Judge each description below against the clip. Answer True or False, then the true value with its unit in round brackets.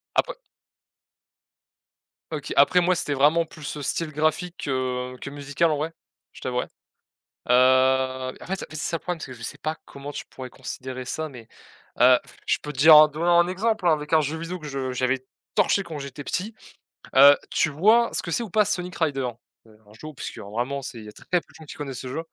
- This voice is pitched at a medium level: True (145 Hz)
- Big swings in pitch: False (4.3 semitones)